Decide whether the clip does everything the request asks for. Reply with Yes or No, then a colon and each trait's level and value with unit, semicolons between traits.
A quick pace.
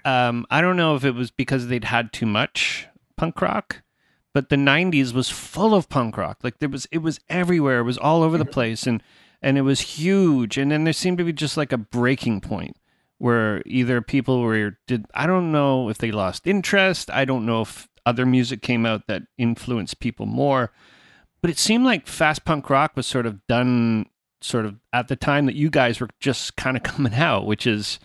Yes: fast, 215 wpm